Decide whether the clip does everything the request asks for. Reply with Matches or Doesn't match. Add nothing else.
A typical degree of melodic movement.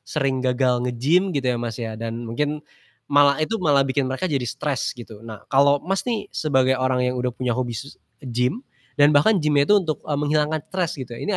Matches